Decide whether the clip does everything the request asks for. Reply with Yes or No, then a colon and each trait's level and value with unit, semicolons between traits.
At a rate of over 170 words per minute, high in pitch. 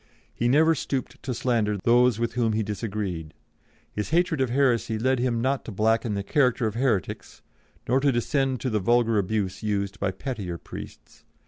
No: average, 180 wpm; low, 115 Hz